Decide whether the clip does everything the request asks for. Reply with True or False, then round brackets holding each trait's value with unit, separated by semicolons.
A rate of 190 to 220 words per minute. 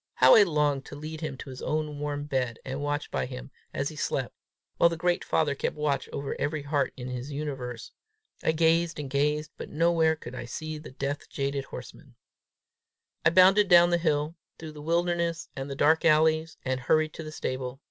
True (200 wpm)